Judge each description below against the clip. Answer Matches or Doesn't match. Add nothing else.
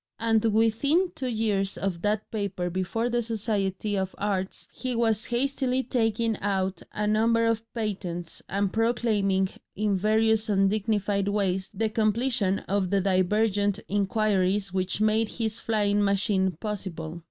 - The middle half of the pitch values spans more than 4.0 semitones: Doesn't match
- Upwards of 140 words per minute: Doesn't match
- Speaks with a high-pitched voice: Matches